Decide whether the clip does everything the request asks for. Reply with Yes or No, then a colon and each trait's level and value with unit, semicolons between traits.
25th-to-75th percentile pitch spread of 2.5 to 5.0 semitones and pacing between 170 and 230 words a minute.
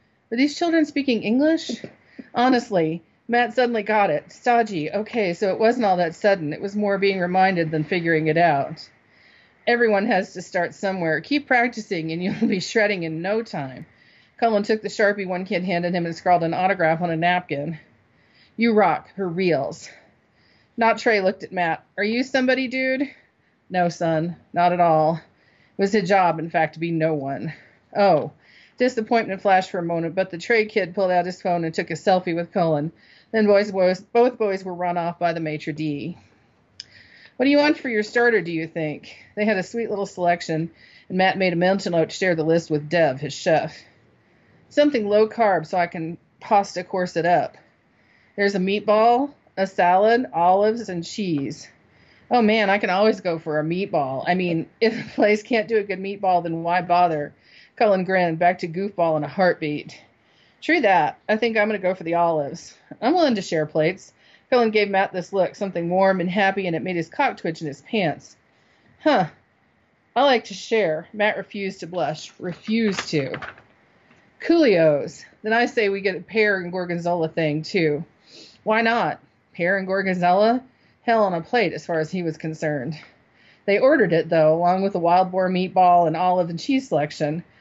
Yes: average, 4.2 semitones; average, 190 wpm